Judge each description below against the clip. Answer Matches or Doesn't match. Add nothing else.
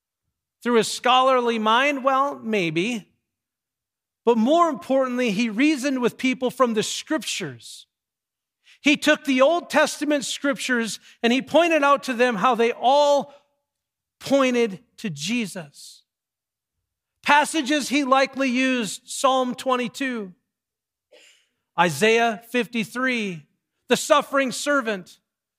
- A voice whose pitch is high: Matches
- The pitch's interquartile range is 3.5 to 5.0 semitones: Matches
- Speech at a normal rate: Doesn't match